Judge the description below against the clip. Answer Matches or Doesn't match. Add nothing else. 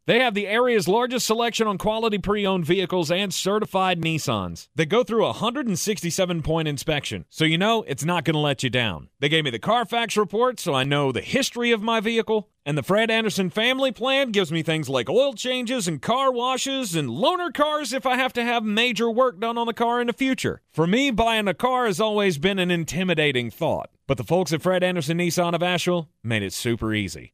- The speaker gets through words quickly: Matches